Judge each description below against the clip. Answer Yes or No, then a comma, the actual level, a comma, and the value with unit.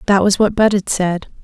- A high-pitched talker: Yes, high, 195 Hz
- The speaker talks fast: Yes, fast, 210 wpm